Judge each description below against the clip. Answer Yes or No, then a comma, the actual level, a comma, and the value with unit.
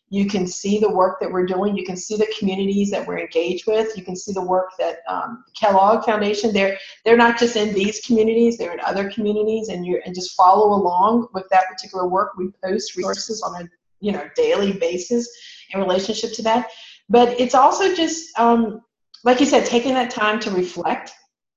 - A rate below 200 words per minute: No, fast, 205 wpm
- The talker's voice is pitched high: Yes, high, 210 Hz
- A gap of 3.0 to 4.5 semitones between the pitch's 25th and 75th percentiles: Yes, average, 3.6 semitones